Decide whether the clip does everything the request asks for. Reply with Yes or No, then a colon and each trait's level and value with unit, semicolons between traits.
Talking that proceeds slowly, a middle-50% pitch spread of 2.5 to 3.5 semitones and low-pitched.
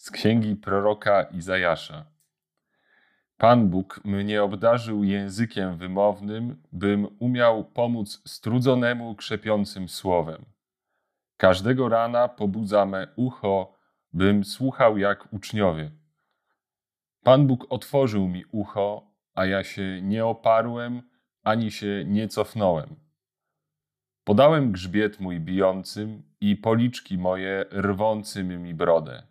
Yes: slow, 100 wpm; average, 2.9 semitones; low, 105 Hz